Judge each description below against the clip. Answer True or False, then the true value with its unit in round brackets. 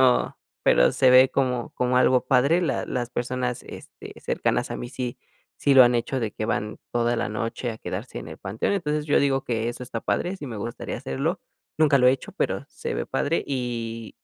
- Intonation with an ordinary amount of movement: False (2.3 semitones)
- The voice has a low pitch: True (125 Hz)